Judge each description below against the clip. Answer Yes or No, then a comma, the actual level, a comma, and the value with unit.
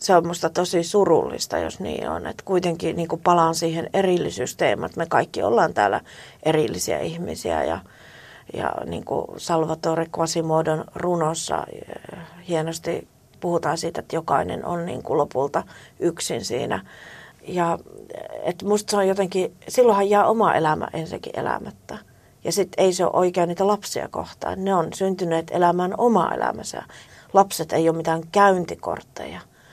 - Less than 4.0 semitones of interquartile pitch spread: Yes, average, 2.8 semitones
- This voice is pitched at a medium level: Yes, medium, 175 Hz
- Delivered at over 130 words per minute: Yes, average, 145 wpm